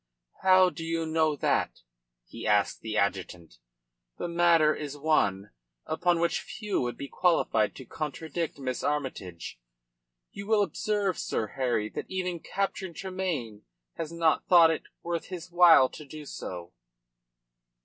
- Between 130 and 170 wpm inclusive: Yes, average, 140 wpm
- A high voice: No, medium, 160 Hz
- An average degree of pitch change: No, wide, 5.7 semitones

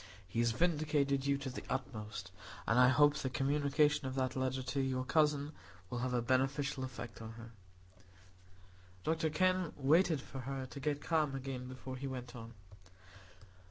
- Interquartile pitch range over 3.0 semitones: No, narrow, 2.6 semitones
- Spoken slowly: No, average, 165 wpm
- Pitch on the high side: No, low, 135 Hz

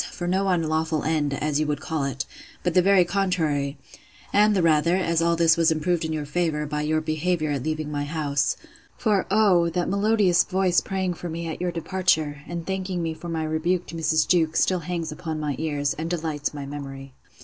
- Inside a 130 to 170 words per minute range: No, fast, 205 wpm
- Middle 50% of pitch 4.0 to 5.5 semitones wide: No, average, 2.9 semitones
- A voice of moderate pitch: Yes, medium, 160 Hz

